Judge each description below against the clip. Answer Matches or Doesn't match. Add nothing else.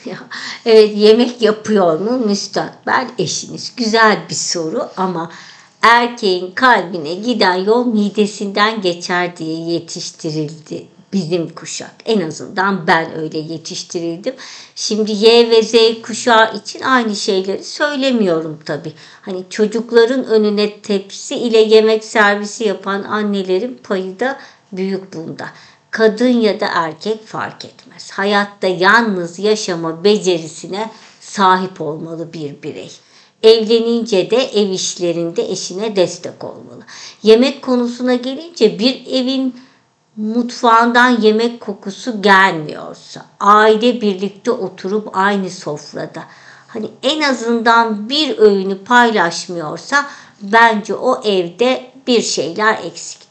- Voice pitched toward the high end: Matches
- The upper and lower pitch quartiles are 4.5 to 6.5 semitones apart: Doesn't match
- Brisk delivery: Doesn't match